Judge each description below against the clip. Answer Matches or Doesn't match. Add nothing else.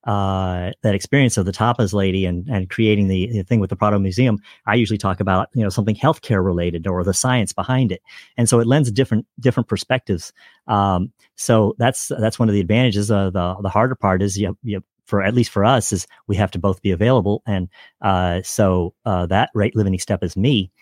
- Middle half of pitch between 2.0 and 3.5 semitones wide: Matches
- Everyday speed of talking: Doesn't match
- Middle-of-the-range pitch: Doesn't match